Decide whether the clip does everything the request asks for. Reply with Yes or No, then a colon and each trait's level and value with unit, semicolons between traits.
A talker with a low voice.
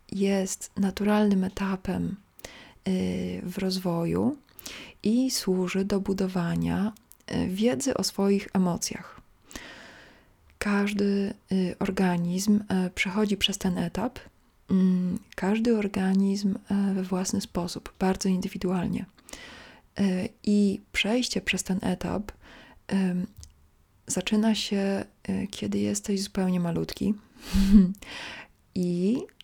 No: high, 195 Hz